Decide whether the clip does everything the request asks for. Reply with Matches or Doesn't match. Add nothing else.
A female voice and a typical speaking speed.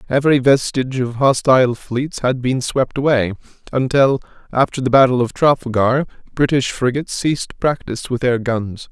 Doesn't match